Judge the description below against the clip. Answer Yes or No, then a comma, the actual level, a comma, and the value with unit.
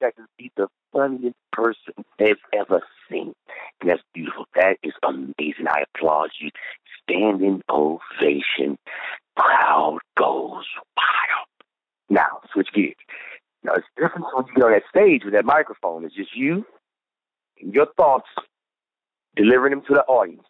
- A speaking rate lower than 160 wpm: Yes, average, 145 wpm